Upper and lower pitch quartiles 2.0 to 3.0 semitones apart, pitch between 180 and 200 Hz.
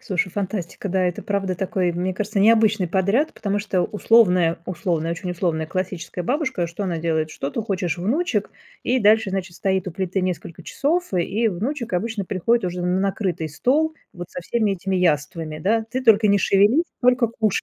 No: average, 3.8 semitones; high, 190 Hz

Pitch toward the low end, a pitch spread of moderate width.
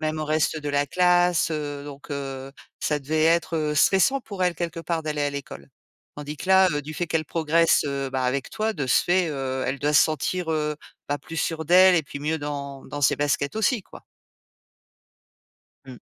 No: medium, 150 Hz; average, 3.0 semitones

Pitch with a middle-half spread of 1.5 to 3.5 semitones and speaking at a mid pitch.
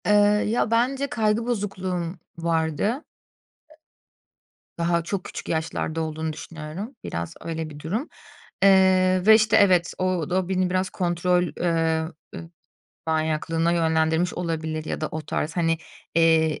Yes: average, 3.0 semitones; medium, 170 Hz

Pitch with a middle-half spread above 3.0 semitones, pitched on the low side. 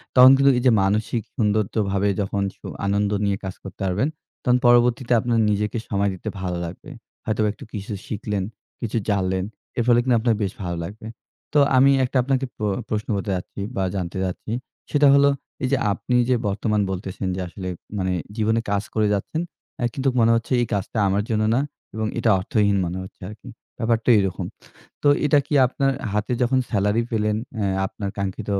Yes: average, 3.6 semitones; low, 105 Hz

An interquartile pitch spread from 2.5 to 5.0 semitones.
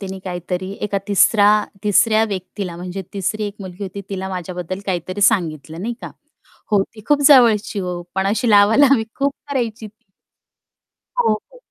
Yes: average, 2.9 semitones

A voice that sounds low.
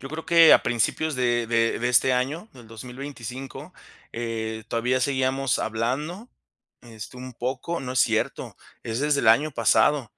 Yes: low, 125 Hz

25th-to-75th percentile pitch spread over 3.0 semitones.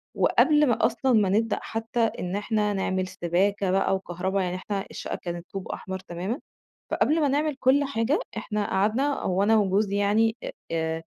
Yes: average, 3.4 semitones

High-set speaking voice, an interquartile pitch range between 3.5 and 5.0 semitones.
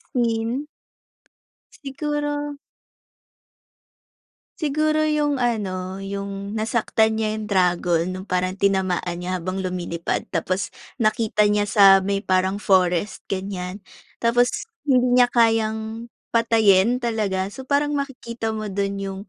Yes: high, 210 Hz; average, 4.1 semitones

